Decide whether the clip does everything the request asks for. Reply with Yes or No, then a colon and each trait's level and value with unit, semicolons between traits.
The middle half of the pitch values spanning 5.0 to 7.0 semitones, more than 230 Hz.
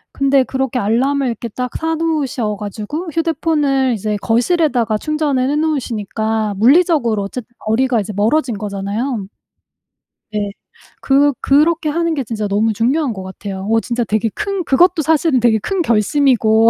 Yes: wide, 5.6 semitones; very high, 250 Hz